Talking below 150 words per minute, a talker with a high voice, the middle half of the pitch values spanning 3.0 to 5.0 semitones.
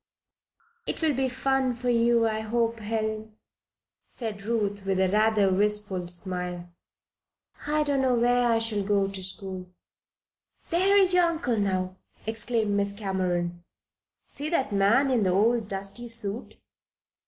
Yes: average, 140 wpm; high, 220 Hz; average, 3.6 semitones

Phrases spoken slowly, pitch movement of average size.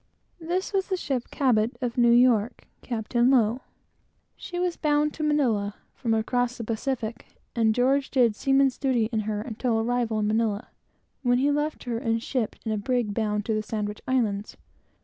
No: average, 180 wpm; average, 3.5 semitones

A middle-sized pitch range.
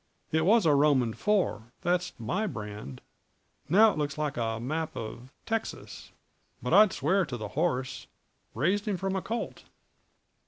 No: wide, 8.1 semitones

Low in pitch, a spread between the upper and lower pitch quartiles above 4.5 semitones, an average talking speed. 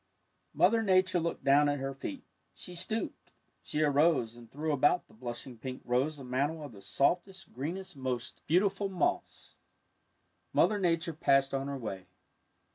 No: medium, 145 Hz; average, 5.3 semitones; average, 160 wpm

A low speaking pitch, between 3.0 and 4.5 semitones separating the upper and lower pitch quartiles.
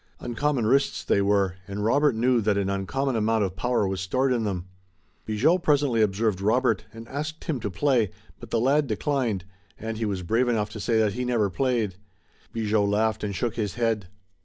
Yes: low, 110 Hz; average, 3.7 semitones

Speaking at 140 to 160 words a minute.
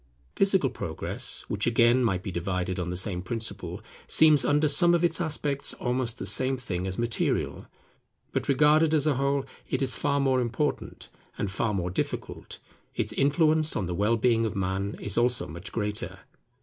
No: average, 175 wpm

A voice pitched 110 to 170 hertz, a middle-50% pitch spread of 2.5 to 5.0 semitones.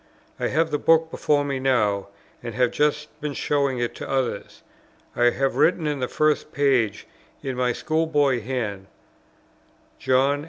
Yes: low, 135 Hz; average, 3.3 semitones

